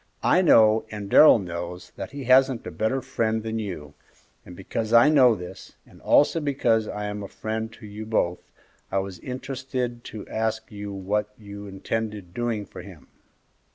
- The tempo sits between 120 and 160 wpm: No, average, 175 wpm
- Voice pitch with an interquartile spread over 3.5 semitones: No, average, 3.1 semitones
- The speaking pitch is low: Yes, low, 110 Hz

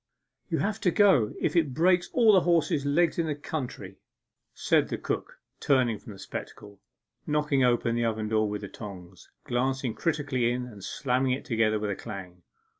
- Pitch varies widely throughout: Yes, wide, 5.9 semitones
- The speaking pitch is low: Yes, low, 125 Hz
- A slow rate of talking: No, average, 185 wpm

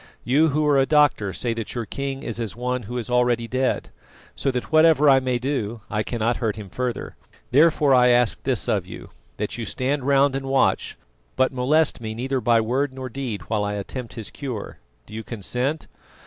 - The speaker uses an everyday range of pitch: Yes, average, 3.1 semitones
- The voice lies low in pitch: Yes, low, 125 Hz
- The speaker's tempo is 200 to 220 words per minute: Yes, fast, 205 wpm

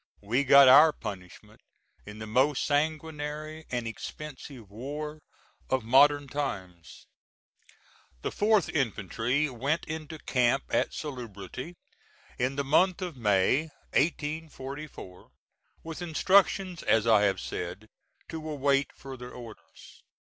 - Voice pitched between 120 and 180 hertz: Yes, medium, 140 Hz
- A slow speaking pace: Yes, slow, 110 wpm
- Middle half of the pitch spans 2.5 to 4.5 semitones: No, average, 5.0 semitones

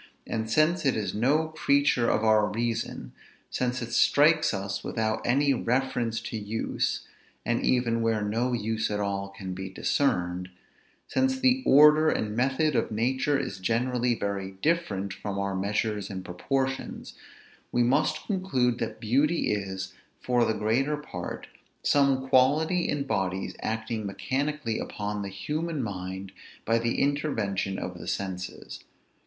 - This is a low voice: Yes, low, 115 Hz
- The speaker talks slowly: No, average, 145 wpm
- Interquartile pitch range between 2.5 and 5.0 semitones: No, wide, 5.4 semitones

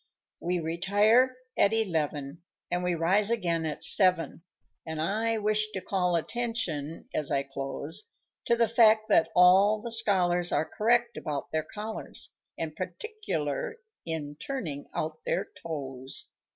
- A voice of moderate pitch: Yes, medium, 180 Hz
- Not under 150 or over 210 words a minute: No, average, 140 wpm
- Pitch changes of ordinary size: No, wide, 5.8 semitones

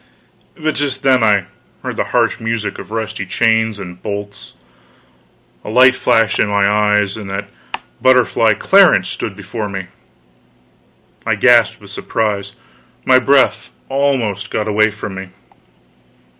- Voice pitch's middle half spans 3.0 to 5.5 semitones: Yes, average, 3.3 semitones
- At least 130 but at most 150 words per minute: Yes, slow, 135 wpm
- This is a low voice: Yes, low, 105 Hz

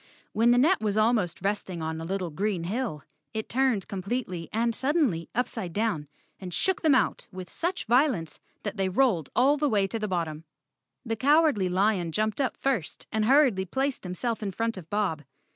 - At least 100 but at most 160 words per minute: No, average, 195 wpm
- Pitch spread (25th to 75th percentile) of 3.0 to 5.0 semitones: No, wide, 5.6 semitones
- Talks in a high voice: Yes, high, 215 Hz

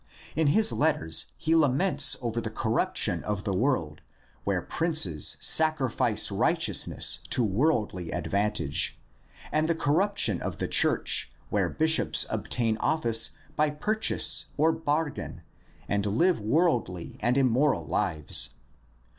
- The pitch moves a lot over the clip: Yes, wide, 7.3 semitones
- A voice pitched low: Yes, low, 130 Hz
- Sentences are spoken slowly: Yes, slow, 120 wpm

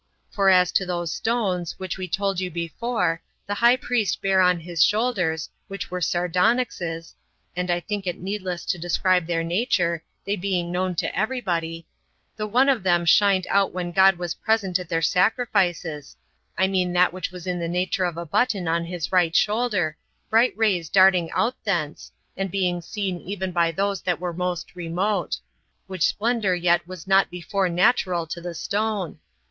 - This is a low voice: No, medium, 180 Hz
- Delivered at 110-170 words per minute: No, average, 180 wpm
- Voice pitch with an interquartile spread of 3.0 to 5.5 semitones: No, narrow, 2.4 semitones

